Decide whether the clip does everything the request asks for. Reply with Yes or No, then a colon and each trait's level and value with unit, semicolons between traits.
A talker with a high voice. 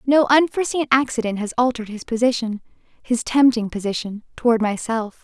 Yes: high, 240 Hz